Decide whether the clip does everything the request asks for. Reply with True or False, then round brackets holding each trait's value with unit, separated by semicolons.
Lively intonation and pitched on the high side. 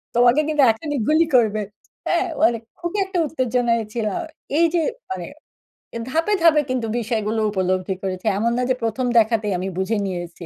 True (6.2 semitones; 235 Hz)